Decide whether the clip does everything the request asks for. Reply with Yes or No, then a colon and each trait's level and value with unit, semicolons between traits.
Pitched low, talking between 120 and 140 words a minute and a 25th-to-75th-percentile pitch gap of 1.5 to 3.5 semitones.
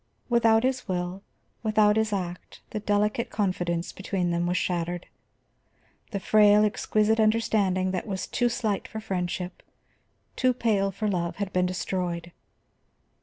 No: high, 200 Hz; slow, 135 wpm; average, 3.2 semitones